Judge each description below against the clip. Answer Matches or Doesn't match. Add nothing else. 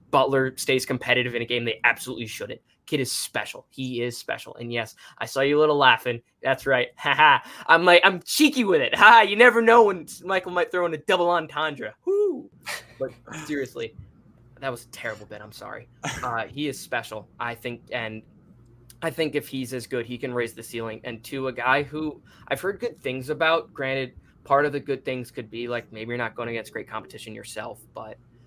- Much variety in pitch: Doesn't match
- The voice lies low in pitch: Matches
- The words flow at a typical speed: Doesn't match